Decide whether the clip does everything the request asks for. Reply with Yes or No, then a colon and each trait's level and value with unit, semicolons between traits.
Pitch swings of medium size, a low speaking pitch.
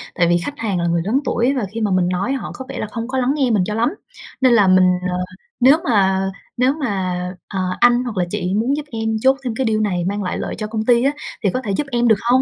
No: average, 4.9 semitones; high, 225 Hz